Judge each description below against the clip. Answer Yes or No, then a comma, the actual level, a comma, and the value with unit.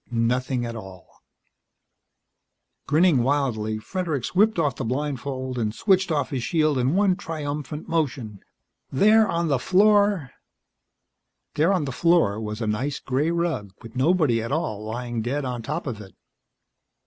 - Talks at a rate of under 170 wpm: Yes, average, 150 wpm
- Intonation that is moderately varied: No, wide, 5.9 semitones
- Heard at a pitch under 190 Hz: Yes, medium, 140 Hz